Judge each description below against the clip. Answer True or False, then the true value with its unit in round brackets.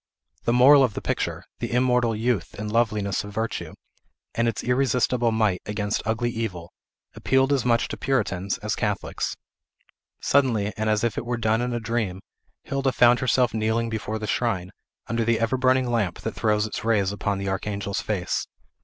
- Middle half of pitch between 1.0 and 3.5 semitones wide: True (2.7 semitones)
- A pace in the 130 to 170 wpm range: False (180 wpm)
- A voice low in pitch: True (115 Hz)